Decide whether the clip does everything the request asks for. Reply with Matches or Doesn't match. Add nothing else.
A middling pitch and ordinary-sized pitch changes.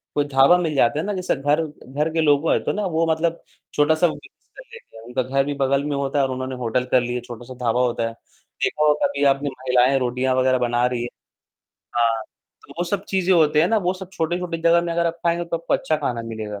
Matches